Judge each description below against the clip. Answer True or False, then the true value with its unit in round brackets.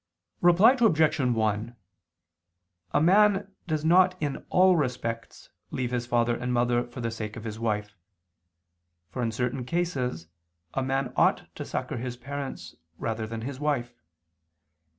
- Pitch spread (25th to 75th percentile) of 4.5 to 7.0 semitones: True (4.8 semitones)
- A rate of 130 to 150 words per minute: True (145 wpm)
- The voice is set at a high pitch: False (125 Hz)